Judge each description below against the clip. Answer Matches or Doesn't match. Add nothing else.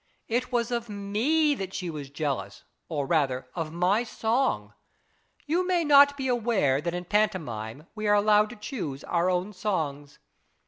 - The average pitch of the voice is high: Matches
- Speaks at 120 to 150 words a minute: Doesn't match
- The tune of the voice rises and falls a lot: Matches